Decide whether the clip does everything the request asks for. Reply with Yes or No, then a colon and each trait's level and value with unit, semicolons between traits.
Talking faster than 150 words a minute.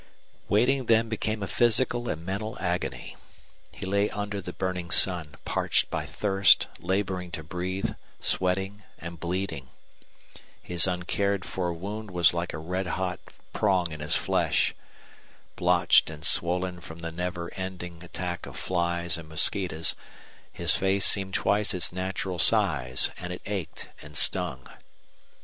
No: average, 140 wpm